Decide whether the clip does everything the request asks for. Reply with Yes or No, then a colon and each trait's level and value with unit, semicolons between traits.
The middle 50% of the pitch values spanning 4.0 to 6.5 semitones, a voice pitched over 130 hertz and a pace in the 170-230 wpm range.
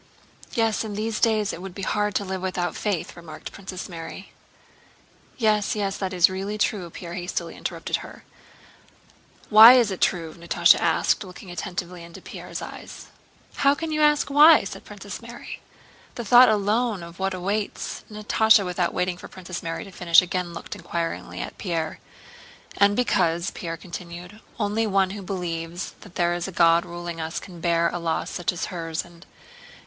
No: average, 3.4 semitones; medium, 185 Hz; average, 175 wpm